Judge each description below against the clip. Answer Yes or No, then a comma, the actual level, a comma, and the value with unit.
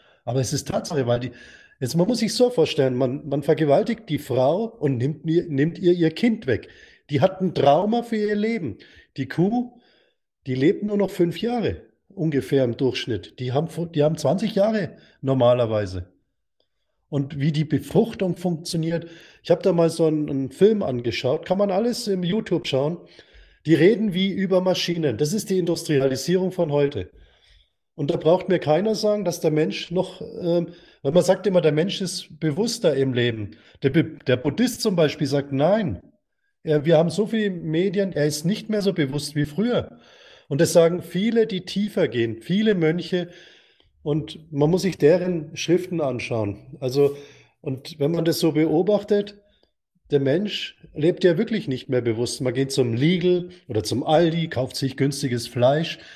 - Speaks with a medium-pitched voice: Yes, medium, 165 Hz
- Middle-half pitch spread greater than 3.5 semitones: Yes, average, 5.1 semitones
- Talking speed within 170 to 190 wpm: Yes, average, 175 wpm